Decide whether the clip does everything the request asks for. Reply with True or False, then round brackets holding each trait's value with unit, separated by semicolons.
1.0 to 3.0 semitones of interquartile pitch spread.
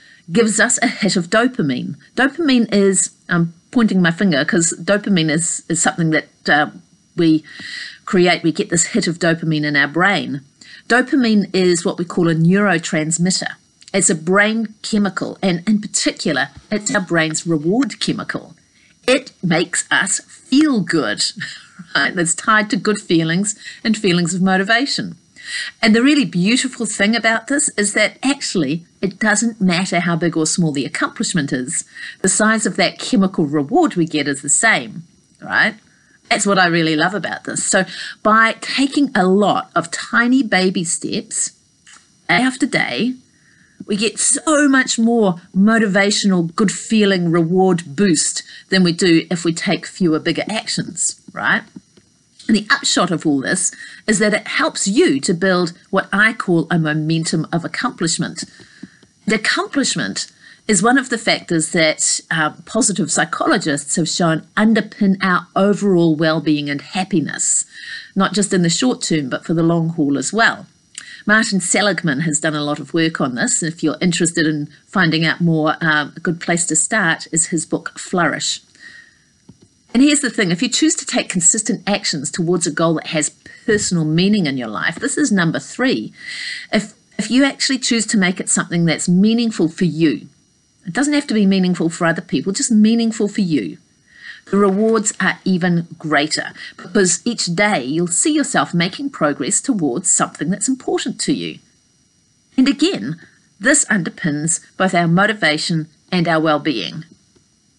False (5.1 semitones)